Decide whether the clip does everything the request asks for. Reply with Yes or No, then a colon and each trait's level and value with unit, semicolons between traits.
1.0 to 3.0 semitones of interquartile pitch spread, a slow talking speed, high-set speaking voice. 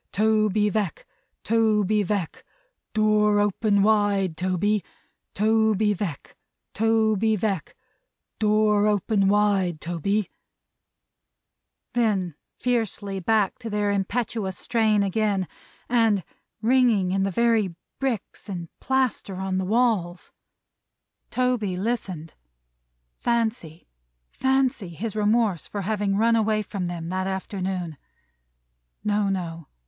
Yes: narrow, 2.6 semitones; slow, 105 wpm; high, 205 Hz